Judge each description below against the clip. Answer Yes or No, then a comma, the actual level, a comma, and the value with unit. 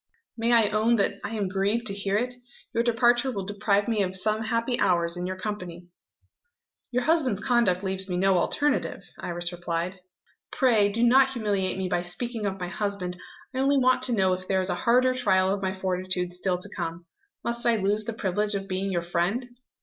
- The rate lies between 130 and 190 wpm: No, fast, 205 wpm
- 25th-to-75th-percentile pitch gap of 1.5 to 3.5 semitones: No, average, 4.1 semitones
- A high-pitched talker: Yes, high, 200 Hz